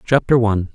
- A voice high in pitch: No, low, 115 Hz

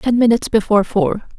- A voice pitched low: No, high, 220 Hz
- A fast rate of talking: No, average, 175 wpm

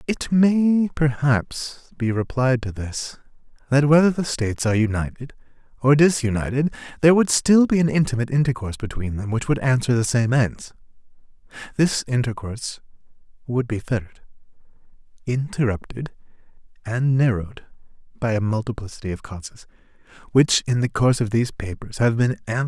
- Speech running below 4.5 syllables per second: No, 5.6 syllables/s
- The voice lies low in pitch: Yes, low, 125 Hz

